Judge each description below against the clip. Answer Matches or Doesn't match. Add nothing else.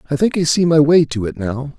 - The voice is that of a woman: Doesn't match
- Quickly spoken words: Matches